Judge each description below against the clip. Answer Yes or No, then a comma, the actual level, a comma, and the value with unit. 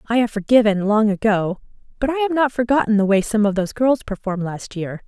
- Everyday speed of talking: No, fast, 225 wpm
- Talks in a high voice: Yes, high, 220 Hz